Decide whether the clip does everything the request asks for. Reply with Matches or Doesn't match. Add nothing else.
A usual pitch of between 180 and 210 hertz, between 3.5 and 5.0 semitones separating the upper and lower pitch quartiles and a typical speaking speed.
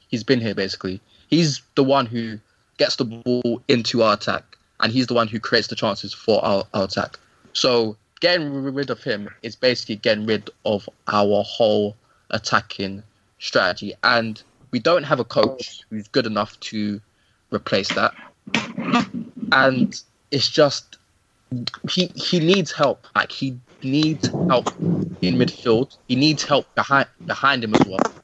Doesn't match